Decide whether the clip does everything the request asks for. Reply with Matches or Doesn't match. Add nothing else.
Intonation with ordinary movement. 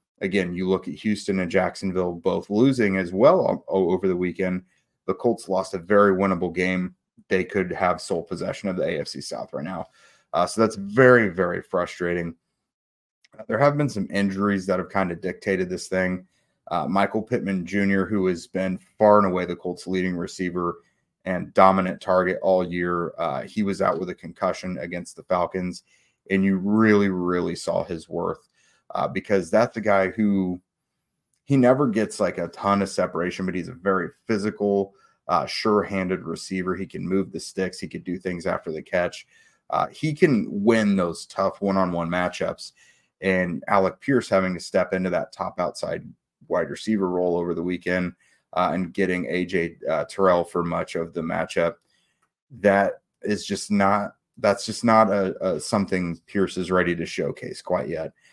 Doesn't match